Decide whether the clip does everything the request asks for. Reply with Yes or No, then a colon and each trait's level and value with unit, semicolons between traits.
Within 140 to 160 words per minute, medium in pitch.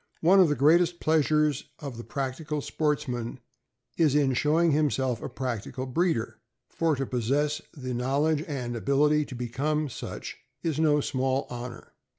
Yes: average, 150 wpm; medium, 145 Hz